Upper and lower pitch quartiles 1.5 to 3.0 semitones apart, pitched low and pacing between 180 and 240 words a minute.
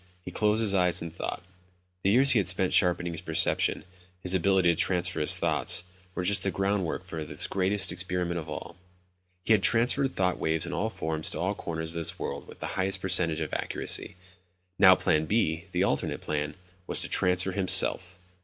Yes: narrow, 2.6 semitones; very low, 90 Hz; average, 195 wpm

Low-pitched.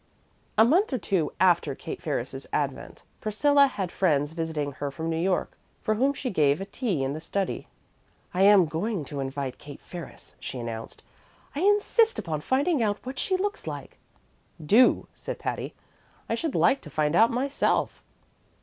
No: high, 190 Hz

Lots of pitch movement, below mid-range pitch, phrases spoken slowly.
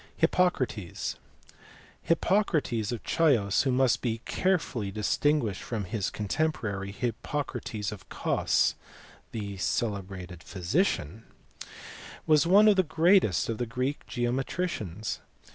Yes: wide, 7.3 semitones; low, 120 Hz; slow, 105 wpm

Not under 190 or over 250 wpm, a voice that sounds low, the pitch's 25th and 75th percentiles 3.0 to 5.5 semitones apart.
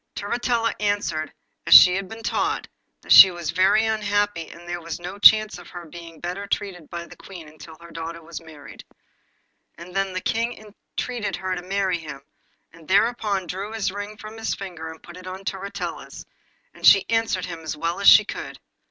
No: average, 200 wpm; medium, 185 Hz; average, 3.4 semitones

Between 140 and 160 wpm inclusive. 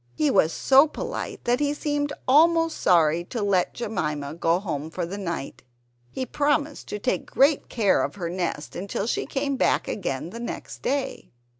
No: average, 175 wpm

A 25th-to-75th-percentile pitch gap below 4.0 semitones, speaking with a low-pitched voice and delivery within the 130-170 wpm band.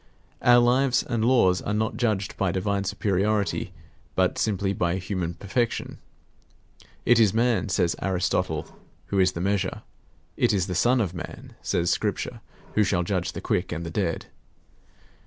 Yes: average, 3.4 semitones; very low, 95 Hz; average, 155 wpm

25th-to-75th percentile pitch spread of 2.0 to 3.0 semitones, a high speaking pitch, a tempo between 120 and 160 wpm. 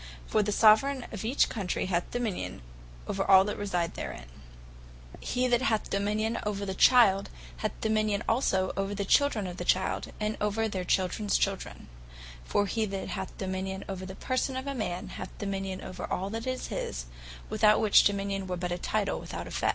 No: narrow, 2.5 semitones; high, 200 Hz; average, 170 wpm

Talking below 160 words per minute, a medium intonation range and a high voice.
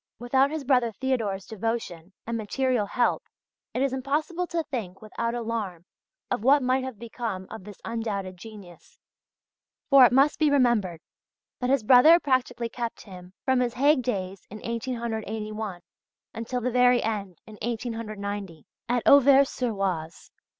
Yes: average, 150 wpm; average, 3.9 semitones; high, 230 Hz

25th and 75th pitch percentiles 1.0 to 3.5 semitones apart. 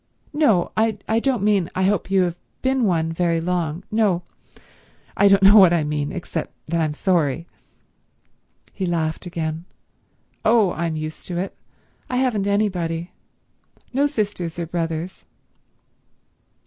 No: average, 3.9 semitones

